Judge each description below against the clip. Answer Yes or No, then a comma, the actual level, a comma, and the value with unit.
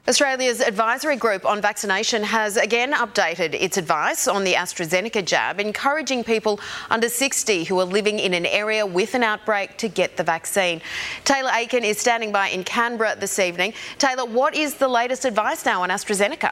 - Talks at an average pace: Yes, average, 180 wpm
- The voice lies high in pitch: Yes, high, 215 Hz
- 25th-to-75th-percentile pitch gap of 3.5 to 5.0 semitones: Yes, average, 4.1 semitones